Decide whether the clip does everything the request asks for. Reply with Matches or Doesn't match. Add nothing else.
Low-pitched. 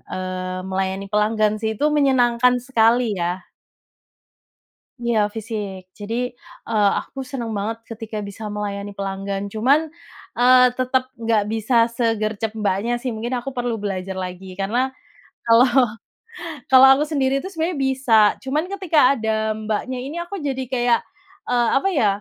Doesn't match